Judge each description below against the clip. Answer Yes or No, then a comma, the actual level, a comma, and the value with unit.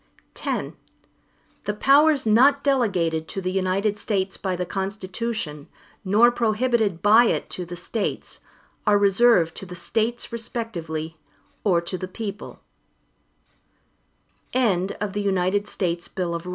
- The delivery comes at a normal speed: No, slow, 105 wpm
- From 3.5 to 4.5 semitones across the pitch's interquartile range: Yes, average, 4.2 semitones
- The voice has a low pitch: No, high, 205 Hz